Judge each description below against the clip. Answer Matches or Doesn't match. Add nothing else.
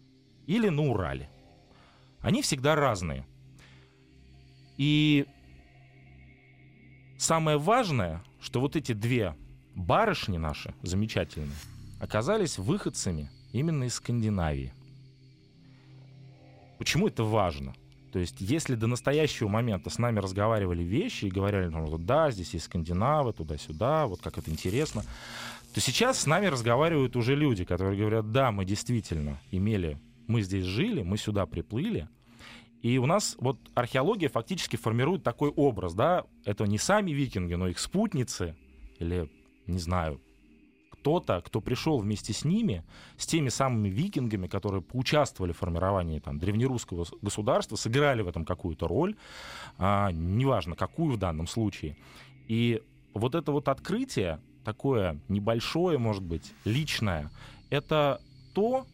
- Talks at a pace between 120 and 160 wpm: Matches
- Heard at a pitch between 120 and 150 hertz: Doesn't match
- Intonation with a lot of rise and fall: Matches